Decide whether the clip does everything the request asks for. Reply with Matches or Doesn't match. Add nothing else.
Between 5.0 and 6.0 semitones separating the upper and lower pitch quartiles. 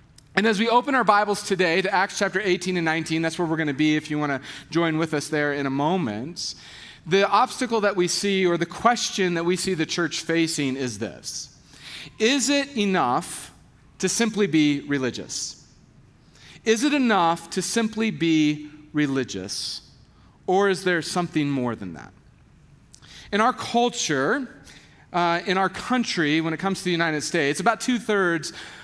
Matches